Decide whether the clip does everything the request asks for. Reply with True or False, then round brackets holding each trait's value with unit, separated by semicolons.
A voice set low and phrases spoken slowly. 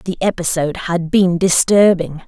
False (180 Hz; 130 wpm)